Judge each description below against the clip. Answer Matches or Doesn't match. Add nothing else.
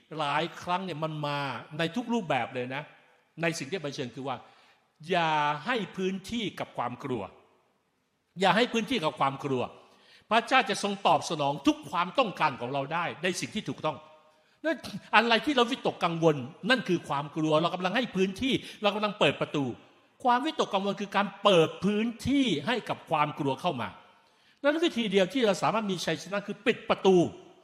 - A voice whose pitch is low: Doesn't match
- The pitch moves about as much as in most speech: Doesn't match